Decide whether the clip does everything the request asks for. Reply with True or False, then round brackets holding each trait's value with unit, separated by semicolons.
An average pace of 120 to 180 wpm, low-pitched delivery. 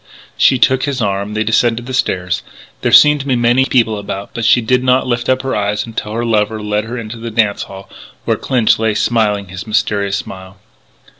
False (205 wpm; 110 Hz)